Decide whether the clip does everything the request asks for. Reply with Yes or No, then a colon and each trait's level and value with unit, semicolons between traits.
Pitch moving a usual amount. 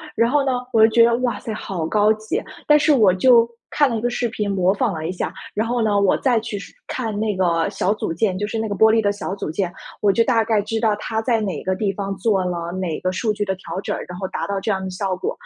Yes: average, 3.2 semitones